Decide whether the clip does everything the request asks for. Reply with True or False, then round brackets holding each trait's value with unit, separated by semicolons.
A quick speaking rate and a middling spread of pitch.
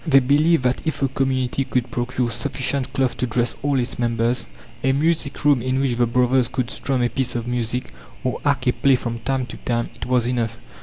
False (215 wpm; 1.9 semitones)